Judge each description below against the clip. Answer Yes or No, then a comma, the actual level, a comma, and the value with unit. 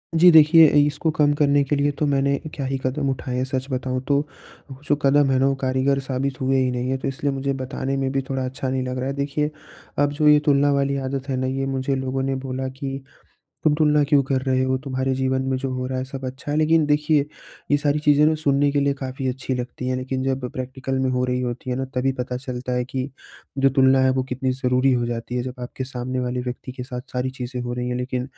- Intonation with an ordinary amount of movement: No, narrow, 1.5 semitones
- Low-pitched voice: Yes, low, 130 Hz